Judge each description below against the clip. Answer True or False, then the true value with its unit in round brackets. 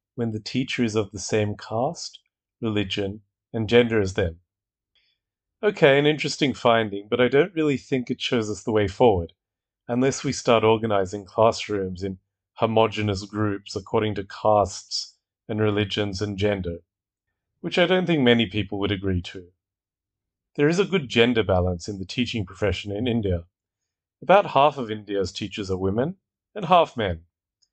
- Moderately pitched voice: False (105 Hz)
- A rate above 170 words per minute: False (160 wpm)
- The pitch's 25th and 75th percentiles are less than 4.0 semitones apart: True (3.4 semitones)